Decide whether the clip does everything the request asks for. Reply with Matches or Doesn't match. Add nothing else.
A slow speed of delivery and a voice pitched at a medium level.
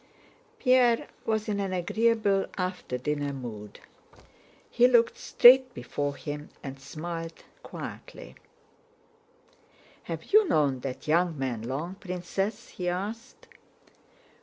Matches